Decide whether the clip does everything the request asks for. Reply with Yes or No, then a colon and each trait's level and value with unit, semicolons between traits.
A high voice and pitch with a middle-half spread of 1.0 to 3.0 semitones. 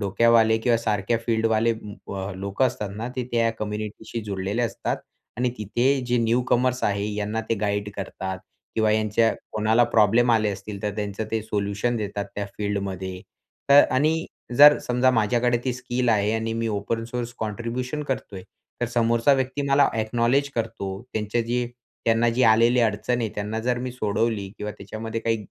No: low, 115 Hz; narrow, 2.6 semitones